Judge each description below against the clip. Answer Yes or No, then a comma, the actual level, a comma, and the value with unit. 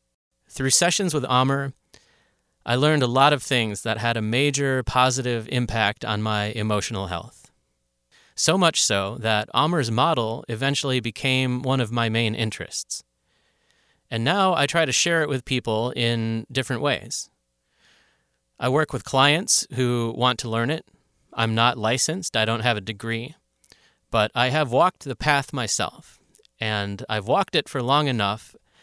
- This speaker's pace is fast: No, average, 160 wpm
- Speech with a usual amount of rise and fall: Yes, average, 3.6 semitones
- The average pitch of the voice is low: Yes, low, 120 Hz